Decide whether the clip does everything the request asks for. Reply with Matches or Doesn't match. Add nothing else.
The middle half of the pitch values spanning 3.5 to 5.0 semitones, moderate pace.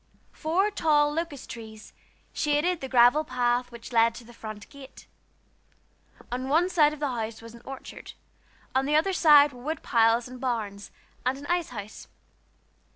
Matches